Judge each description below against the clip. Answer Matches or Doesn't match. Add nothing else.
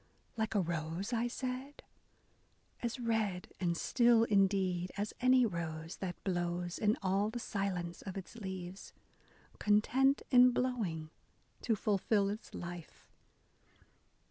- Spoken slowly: Matches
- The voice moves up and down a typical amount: Matches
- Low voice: Doesn't match